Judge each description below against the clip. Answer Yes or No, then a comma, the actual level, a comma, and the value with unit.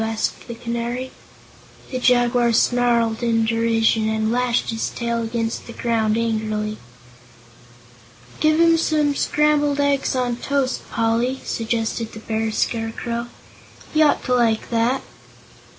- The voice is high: Yes, high, 235 Hz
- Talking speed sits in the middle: No, slow, 125 wpm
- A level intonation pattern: Yes, narrow, 2.0 semitones